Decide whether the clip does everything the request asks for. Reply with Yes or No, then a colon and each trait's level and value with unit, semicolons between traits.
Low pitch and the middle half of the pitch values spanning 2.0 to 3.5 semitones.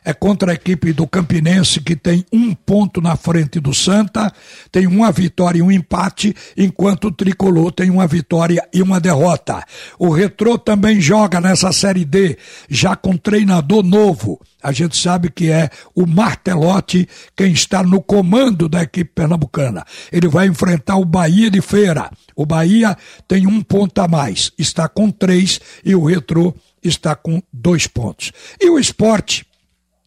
No: medium, 180 Hz; average, 2.7 semitones